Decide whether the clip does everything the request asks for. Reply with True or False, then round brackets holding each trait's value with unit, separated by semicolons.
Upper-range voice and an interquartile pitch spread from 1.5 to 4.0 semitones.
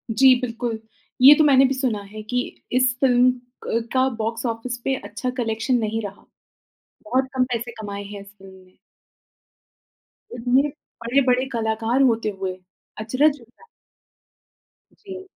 True (240 Hz; 2.8 semitones)